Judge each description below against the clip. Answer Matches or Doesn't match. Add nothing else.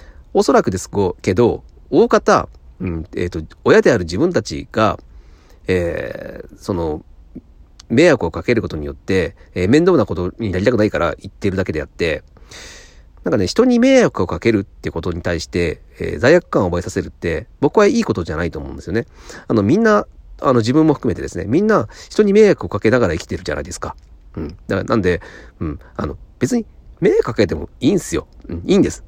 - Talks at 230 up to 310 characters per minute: Doesn't match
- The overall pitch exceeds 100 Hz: Doesn't match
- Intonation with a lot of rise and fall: Matches